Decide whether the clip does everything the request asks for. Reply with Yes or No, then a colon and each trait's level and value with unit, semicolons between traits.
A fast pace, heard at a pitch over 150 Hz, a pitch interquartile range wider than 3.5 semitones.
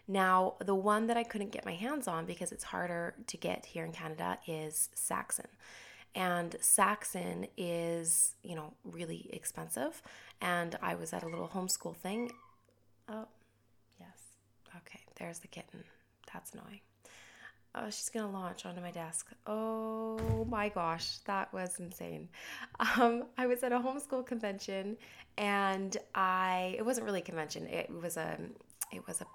No: average, 155 wpm; medium, 185 Hz; average, 4.6 semitones